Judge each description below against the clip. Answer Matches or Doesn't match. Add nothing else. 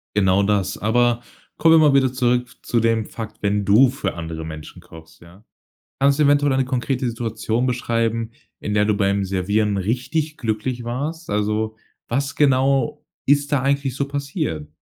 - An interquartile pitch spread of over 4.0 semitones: Matches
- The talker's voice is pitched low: Matches